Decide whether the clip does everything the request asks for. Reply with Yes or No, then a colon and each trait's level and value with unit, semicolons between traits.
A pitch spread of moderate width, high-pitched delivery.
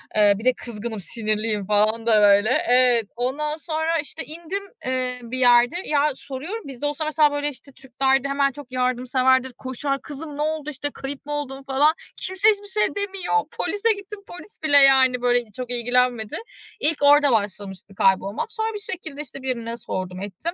Yes: average, 4.2 semitones; very high, 265 Hz